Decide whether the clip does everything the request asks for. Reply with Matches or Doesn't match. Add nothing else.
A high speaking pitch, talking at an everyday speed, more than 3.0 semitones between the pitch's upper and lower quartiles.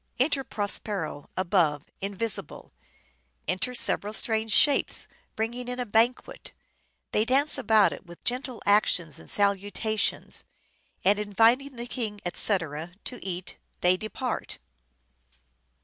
Doesn't match